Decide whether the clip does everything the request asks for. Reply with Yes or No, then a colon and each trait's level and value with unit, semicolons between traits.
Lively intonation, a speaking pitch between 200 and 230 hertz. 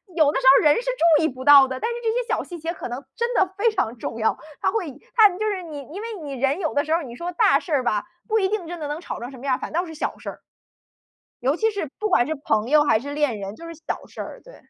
No: wide, 6.1 semitones; very high, 310 Hz